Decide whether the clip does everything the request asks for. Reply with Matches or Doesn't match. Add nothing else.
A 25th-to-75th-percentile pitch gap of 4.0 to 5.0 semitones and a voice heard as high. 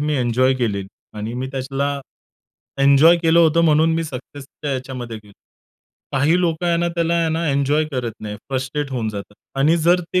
Doesn't match